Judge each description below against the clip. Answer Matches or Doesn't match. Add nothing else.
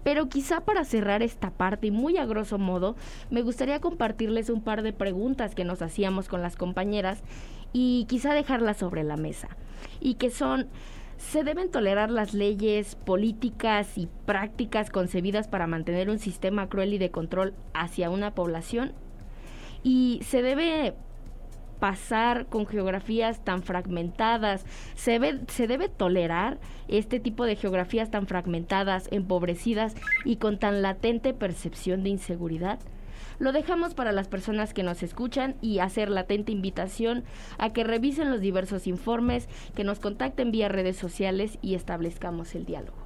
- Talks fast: Doesn't match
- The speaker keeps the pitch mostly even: Doesn't match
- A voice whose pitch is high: Matches